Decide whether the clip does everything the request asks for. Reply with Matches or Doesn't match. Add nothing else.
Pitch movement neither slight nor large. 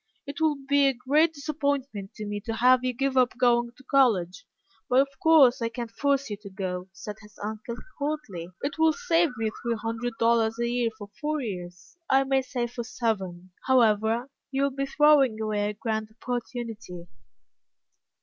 Matches